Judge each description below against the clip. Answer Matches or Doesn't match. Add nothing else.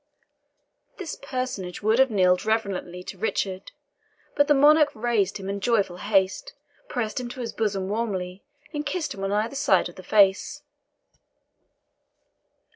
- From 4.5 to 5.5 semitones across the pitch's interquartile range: Matches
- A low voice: Doesn't match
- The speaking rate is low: Doesn't match